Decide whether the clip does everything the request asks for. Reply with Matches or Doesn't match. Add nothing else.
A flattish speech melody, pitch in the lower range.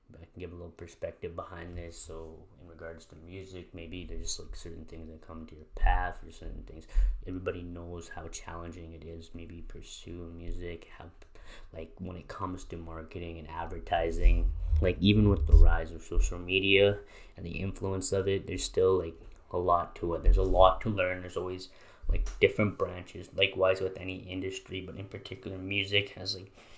Matches